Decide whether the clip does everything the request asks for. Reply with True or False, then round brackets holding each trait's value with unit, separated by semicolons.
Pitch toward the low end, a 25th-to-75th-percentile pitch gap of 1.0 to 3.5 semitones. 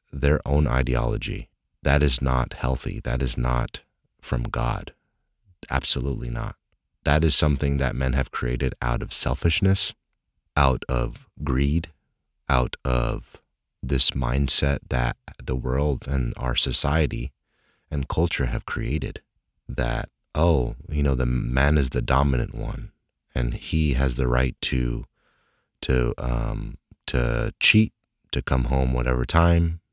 True (70 Hz; 3.2 semitones)